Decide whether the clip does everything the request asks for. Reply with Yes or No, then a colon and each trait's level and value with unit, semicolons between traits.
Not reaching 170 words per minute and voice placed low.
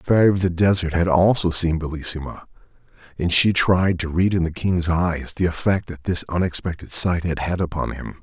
No: fast, 205 wpm; very low, 85 Hz